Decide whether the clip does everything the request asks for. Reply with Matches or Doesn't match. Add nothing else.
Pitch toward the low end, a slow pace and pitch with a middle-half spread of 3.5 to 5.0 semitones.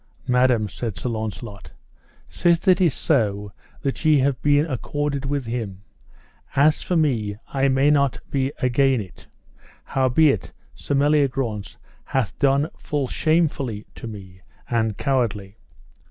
Matches